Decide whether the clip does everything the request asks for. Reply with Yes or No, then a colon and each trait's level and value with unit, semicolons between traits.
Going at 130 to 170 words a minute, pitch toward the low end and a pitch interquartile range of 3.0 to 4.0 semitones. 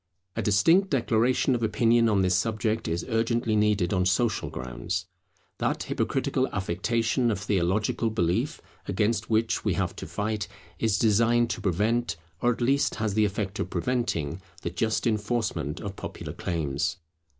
Yes: average, 150 wpm; low, 110 Hz; average, 3.7 semitones